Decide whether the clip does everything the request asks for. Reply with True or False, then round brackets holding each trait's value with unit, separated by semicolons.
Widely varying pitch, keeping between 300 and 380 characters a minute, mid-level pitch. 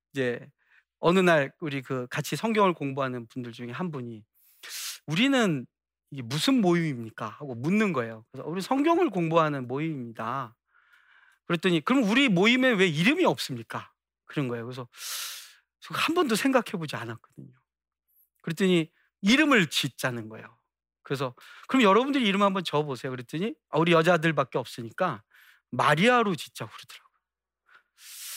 True (8.1 semitones; 335 characters per minute; 155 Hz)